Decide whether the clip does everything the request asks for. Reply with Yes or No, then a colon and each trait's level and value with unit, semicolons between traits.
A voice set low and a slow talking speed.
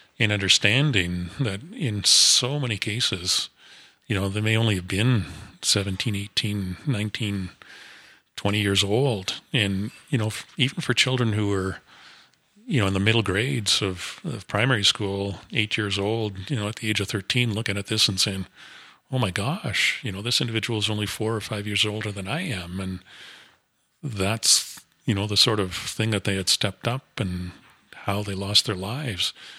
No: low, 105 Hz; average, 185 wpm